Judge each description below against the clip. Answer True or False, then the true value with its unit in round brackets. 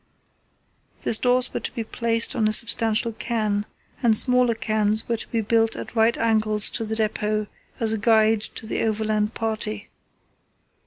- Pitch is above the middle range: True (220 Hz)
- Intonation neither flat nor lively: False (1.2 semitones)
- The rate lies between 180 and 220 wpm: False (165 wpm)